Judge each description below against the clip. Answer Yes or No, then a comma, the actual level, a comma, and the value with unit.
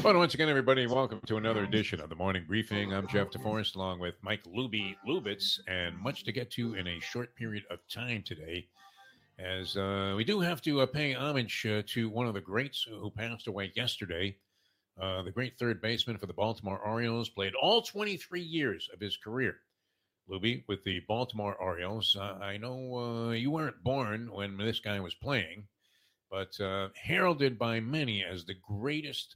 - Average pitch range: Yes, average, 4.3 semitones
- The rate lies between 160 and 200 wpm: Yes, average, 190 wpm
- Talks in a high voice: No, low, 110 Hz